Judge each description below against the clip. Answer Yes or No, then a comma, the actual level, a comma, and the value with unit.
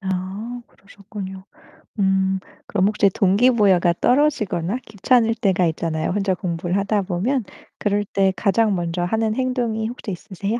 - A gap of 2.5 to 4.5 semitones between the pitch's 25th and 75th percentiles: Yes, average, 2.9 semitones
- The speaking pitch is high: Yes, high, 200 Hz